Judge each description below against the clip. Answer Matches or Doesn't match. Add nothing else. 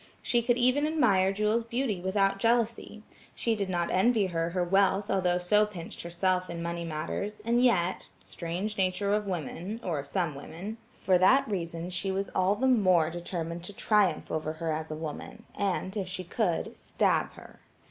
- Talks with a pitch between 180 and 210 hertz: Matches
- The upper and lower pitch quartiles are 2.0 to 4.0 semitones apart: Matches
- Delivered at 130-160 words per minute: Doesn't match